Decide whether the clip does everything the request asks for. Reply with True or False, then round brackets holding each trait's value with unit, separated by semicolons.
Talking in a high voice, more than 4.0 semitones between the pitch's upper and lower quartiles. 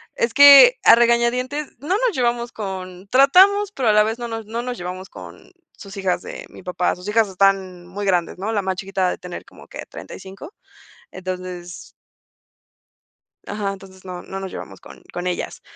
True (200 Hz; 4.4 semitones)